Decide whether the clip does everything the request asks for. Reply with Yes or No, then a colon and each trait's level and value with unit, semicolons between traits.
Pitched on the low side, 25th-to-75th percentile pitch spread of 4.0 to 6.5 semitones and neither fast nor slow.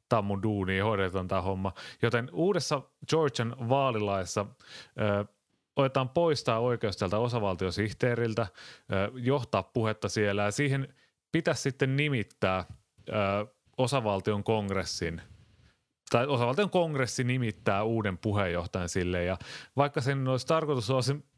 Yes: low, 115 Hz; average, 4.9 semitones; average, 115 wpm